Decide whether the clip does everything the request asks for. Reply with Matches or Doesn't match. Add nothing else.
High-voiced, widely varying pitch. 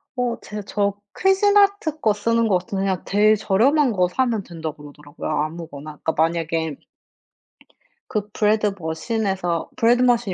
Matches